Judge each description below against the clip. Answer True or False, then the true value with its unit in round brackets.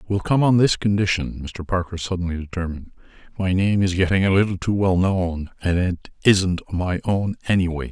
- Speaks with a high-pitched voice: False (90 Hz)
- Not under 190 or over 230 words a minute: False (180 wpm)